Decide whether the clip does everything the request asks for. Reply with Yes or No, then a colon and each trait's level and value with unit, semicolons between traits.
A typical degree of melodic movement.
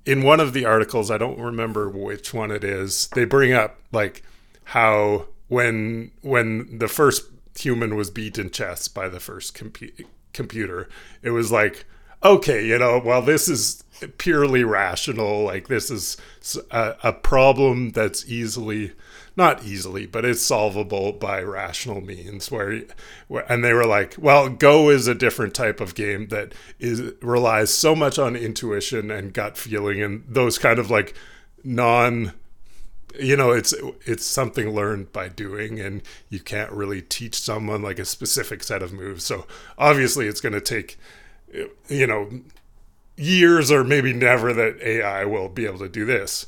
Yes: average, 3.6 semitones